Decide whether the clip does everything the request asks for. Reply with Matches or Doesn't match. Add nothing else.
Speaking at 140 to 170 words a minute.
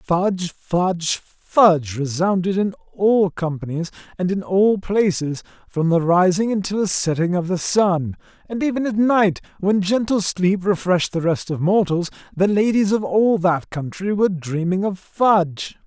Matches